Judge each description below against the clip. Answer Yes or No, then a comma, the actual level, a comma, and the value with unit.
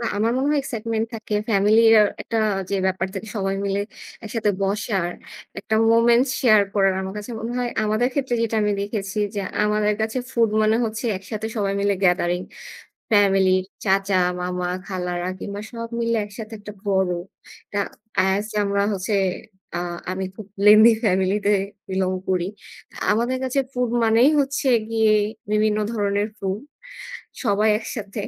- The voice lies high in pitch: Yes, high, 210 Hz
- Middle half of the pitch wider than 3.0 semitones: No, narrow, 2.5 semitones